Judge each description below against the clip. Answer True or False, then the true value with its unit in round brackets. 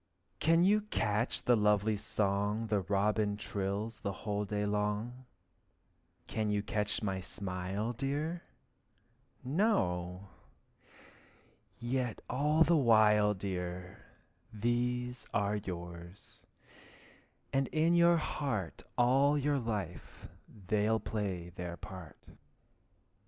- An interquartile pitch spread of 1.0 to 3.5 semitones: False (4.1 semitones)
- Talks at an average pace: False (100 wpm)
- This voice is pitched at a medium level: False (105 Hz)